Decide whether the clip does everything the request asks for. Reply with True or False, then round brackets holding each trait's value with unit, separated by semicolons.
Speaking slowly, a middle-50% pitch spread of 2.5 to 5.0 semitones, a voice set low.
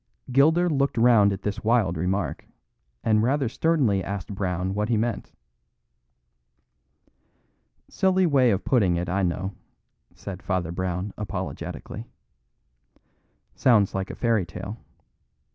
True (120 wpm; 4.6 semitones; 105 Hz)